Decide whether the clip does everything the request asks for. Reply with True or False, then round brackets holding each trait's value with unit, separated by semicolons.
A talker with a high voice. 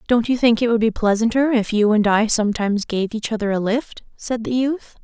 True (225 Hz)